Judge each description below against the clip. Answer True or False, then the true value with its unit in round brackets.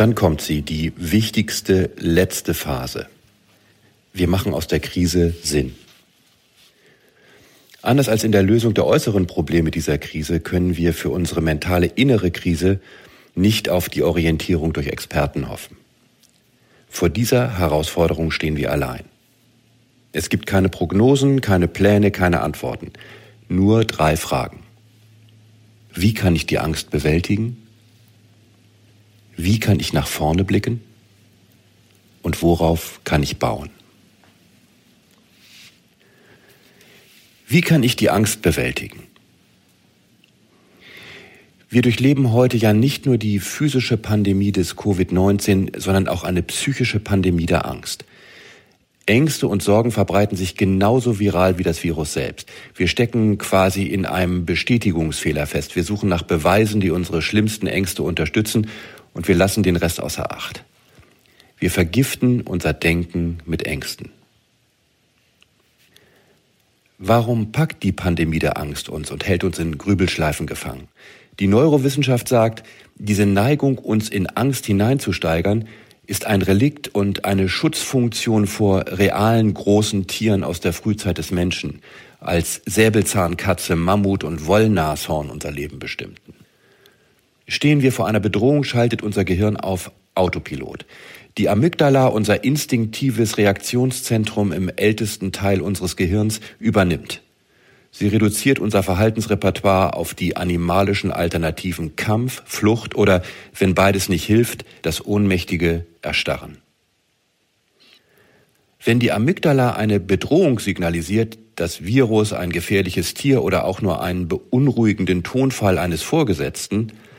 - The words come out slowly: True (120 wpm)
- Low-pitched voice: True (100 Hz)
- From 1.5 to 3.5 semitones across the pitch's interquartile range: False (4.1 semitones)